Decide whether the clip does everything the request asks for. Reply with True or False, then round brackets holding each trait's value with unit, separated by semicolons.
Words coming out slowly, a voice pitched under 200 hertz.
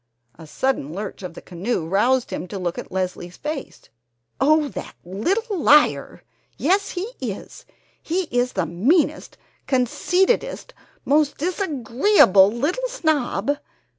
False (125 wpm; 270 Hz)